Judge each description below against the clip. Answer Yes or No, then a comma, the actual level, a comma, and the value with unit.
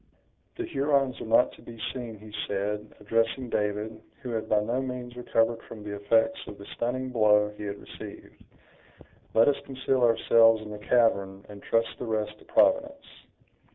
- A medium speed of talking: Yes, average, 175 wpm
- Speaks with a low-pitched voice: Yes, low, 115 Hz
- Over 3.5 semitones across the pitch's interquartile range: No, average, 2.9 semitones